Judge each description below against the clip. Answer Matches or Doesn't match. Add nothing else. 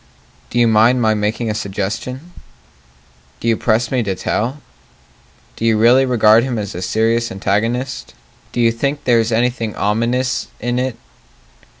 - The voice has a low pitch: Matches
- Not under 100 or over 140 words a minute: Doesn't match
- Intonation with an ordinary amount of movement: Doesn't match